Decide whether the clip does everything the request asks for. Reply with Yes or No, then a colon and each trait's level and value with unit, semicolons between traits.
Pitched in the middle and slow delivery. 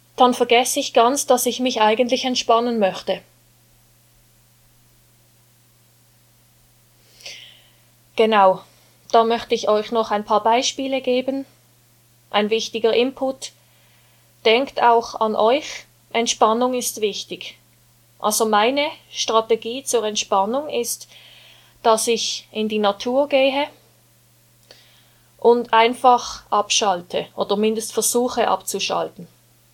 No: high, 215 Hz; slow, 100 wpm